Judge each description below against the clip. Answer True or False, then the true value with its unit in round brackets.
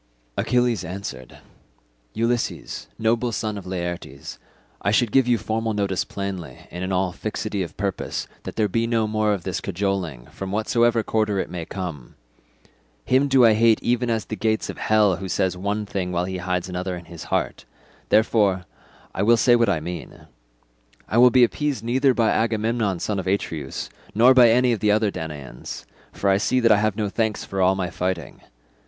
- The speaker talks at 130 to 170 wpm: False (190 wpm)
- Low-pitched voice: True (105 Hz)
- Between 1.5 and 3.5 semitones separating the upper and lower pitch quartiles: False (3.9 semitones)